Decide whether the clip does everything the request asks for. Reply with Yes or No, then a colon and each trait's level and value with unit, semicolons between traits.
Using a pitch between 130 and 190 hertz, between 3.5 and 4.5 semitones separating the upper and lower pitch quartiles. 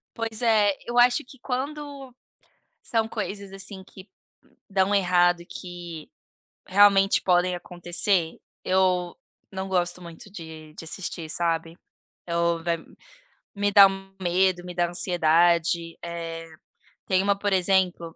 No: medium, 185 Hz; average, 2.8 semitones